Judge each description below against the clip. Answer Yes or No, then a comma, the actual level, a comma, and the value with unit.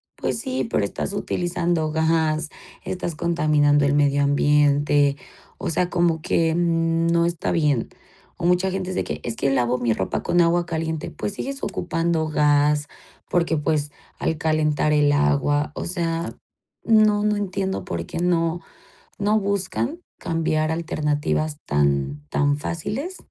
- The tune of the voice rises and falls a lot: No, average, 3.1 semitones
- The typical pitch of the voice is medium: Yes, medium, 160 Hz